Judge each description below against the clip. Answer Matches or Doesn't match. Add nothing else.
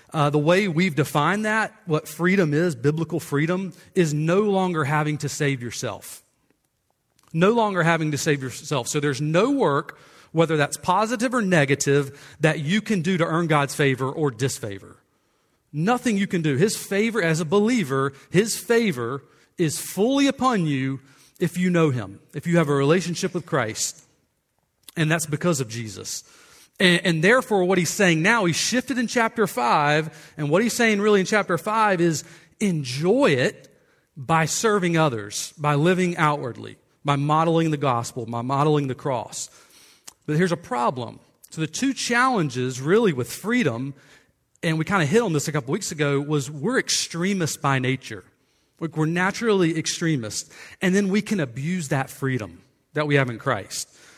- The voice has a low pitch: Doesn't match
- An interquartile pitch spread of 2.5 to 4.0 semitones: Doesn't match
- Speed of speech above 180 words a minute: Doesn't match